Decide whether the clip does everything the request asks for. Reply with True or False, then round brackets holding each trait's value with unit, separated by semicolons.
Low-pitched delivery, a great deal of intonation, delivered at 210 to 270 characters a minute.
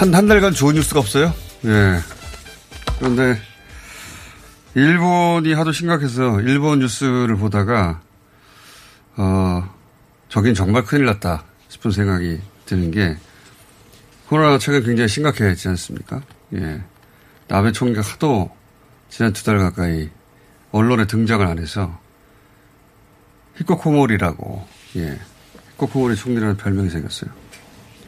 True (110 Hz; 5.8 semitones; 250 characters per minute)